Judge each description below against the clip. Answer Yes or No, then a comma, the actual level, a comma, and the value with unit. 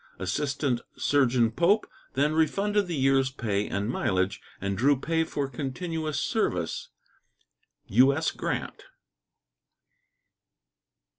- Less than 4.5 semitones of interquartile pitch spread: No, average, 5.1 semitones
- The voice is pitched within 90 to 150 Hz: Yes, medium, 140 Hz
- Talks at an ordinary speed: No, slow, 95 wpm